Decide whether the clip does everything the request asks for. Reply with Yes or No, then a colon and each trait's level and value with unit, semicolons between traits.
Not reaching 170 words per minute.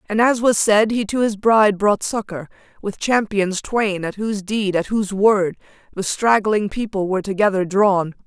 No: average, 180 wpm